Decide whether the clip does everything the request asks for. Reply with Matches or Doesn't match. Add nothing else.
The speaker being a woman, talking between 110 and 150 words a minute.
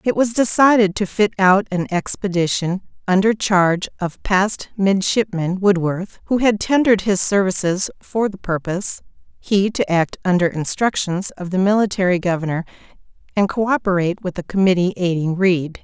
Matches